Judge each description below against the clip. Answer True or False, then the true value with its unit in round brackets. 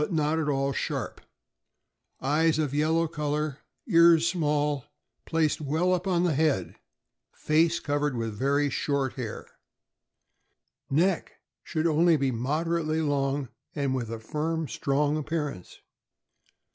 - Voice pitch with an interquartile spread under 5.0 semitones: True (2.8 semitones)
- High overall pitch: False (150 Hz)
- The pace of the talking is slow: True (125 wpm)